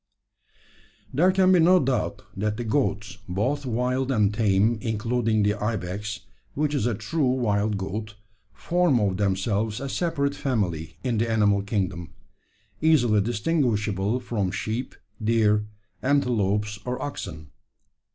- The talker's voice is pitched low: Yes, low, 110 Hz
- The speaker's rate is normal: No, slow, 130 wpm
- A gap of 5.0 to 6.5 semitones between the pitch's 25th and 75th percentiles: No, average, 4.0 semitones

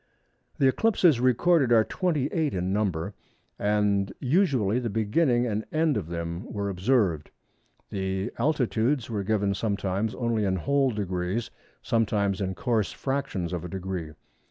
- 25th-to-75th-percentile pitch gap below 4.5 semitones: No, average, 5.0 semitones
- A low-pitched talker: Yes, low, 105 Hz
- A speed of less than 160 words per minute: Yes, slow, 135 wpm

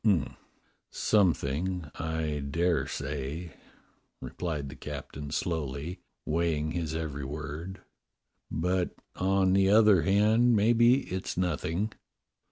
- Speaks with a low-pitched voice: Yes, very low, 85 Hz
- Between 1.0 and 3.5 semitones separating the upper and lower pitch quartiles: No, average, 4.2 semitones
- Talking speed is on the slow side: Yes, slow, 100 wpm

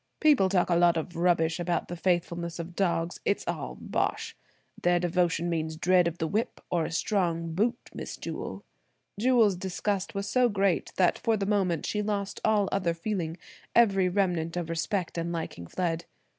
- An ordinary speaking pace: Yes, average, 175 wpm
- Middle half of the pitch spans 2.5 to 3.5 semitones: Yes, average, 2.9 semitones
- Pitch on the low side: No, medium, 175 Hz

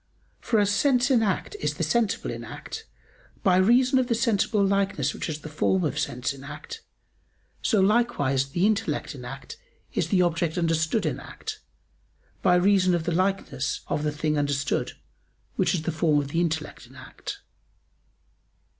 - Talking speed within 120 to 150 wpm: No, average, 170 wpm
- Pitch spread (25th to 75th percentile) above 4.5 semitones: Yes, wide, 5.6 semitones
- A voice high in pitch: No, medium, 180 Hz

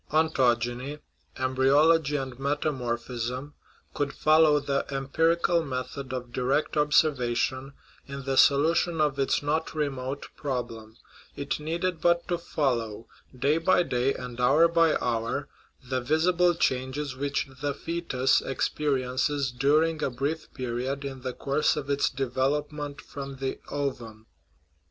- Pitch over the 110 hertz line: Yes, medium, 140 Hz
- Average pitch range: Yes, average, 3.0 semitones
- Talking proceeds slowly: Yes, slow, 130 wpm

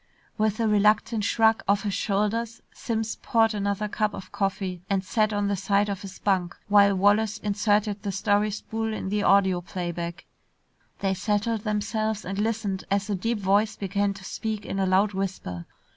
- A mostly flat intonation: Yes, narrow, 1.7 semitones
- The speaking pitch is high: Yes, high, 205 Hz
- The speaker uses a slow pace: No, average, 175 wpm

